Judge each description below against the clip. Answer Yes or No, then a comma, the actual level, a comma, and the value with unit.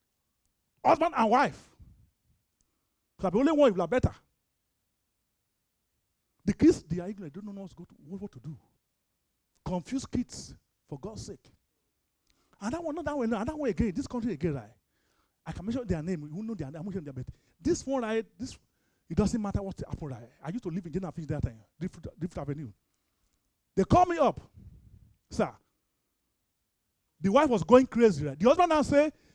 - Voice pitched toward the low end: No, high, 195 Hz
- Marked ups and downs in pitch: Yes, wide, 8.3 semitones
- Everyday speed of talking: Yes, average, 195 wpm